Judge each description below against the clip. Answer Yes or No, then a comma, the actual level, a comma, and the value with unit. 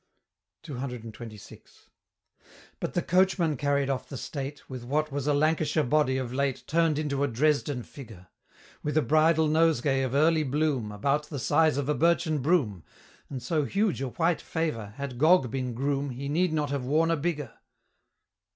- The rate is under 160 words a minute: No, average, 170 wpm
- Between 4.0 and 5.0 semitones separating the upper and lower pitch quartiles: No, average, 3.1 semitones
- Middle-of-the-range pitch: Yes, medium, 145 Hz